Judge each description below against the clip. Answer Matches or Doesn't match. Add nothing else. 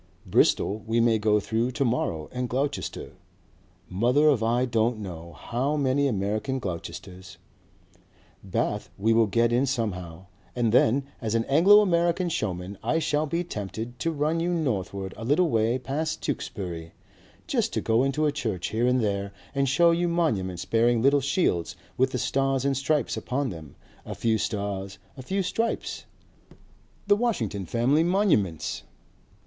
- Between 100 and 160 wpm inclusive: Matches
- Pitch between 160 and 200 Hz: Doesn't match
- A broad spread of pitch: Matches